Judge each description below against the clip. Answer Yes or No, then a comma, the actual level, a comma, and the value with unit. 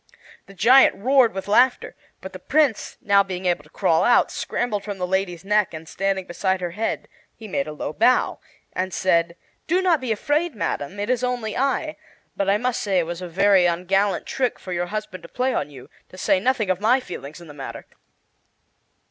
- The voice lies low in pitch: No, high, 195 Hz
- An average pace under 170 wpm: No, fast, 205 wpm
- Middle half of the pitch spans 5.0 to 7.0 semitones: Yes, wide, 5.4 semitones